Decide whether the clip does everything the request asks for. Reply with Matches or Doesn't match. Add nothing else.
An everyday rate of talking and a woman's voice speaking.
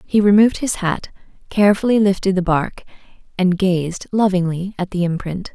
Matches